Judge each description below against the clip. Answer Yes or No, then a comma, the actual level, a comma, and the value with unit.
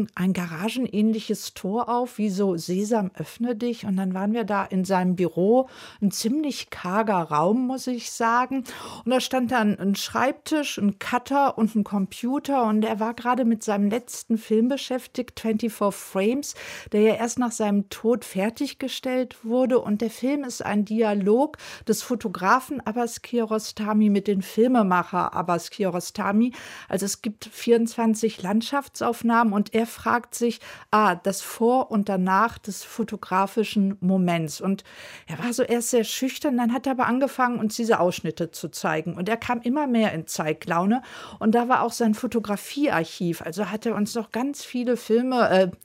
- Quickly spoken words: No, average, 165 wpm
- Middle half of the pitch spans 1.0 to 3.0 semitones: No, average, 3.5 semitones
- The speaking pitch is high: Yes, high, 225 Hz